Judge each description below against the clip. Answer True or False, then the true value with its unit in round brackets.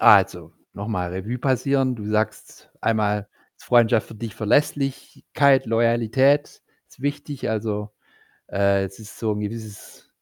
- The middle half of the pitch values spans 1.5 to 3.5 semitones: False (3.9 semitones)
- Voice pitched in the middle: False (110 Hz)